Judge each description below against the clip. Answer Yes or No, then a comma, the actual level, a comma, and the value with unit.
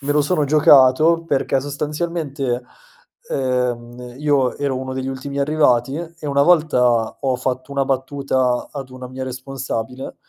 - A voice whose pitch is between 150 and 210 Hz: No, low, 135 Hz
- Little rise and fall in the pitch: Yes, narrow, 2.2 semitones